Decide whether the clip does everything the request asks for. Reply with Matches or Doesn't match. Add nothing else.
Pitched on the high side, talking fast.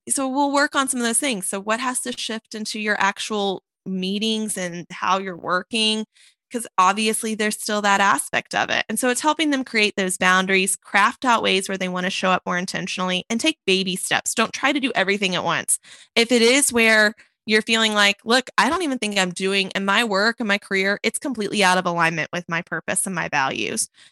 Matches